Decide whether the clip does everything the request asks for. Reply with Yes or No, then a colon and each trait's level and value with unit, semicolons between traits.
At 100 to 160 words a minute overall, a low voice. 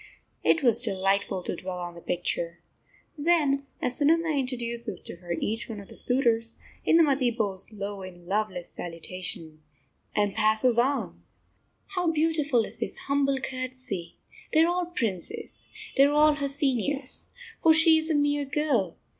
No: average, 155 wpm; high, 245 Hz